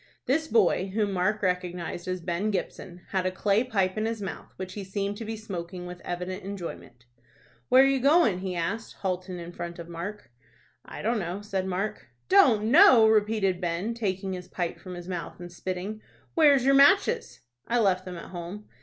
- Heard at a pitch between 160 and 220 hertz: Yes, high, 190 Hz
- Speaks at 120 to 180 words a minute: No, average, 190 wpm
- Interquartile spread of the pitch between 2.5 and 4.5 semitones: Yes, average, 3.6 semitones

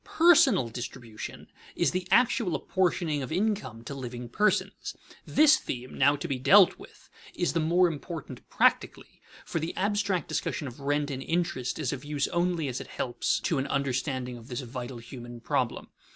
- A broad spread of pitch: Yes, wide, 5.9 semitones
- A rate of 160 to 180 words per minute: Yes, average, 170 wpm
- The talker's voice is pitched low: No, medium, 145 Hz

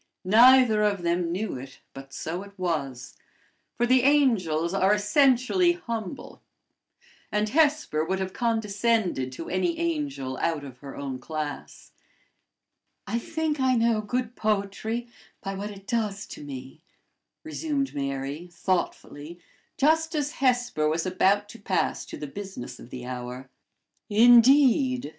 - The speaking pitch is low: No, high, 205 Hz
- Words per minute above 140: No, slow, 135 wpm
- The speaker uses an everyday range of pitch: No, wide, 8.0 semitones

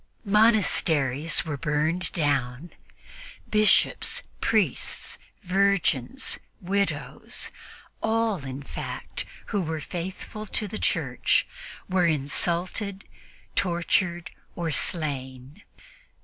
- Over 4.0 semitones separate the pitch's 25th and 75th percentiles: Yes, average, 5.1 semitones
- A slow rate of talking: Yes, slow, 80 wpm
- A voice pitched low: No, medium, 175 Hz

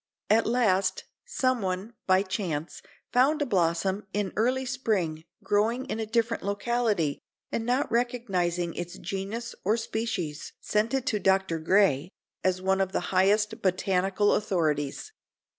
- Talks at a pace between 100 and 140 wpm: Yes, slow, 135 wpm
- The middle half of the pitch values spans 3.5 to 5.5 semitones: Yes, average, 4.1 semitones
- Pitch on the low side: No, high, 200 Hz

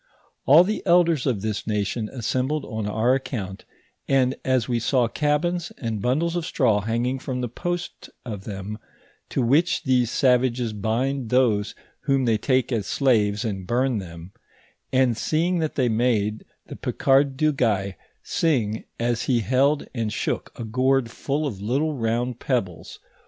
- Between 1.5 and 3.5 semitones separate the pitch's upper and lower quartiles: No, average, 3.9 semitones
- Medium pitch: No, low, 125 Hz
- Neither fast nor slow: Yes, average, 160 wpm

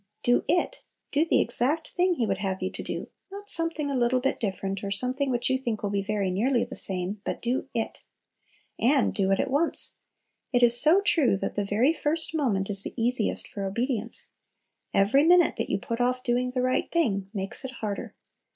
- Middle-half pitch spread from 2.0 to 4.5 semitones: No, wide, 5.5 semitones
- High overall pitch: Yes, high, 245 Hz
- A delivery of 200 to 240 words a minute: Yes, fast, 205 wpm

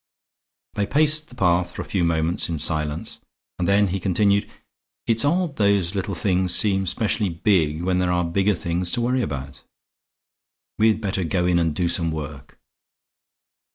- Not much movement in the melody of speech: No, average, 3.6 semitones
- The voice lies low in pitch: Yes, very low, 90 Hz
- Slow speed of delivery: No, average, 165 wpm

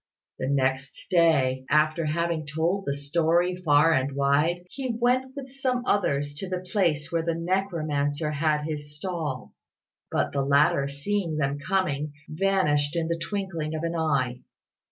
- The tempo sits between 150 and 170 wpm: Yes, average, 155 wpm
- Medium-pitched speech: Yes, medium, 155 Hz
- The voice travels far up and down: No, average, 4.0 semitones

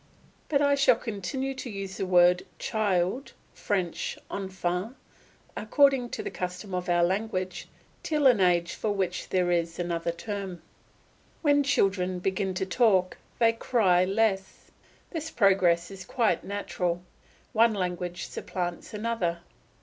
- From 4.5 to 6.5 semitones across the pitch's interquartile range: No, average, 3.9 semitones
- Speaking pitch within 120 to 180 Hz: No, high, 190 Hz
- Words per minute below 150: Yes, slow, 135 wpm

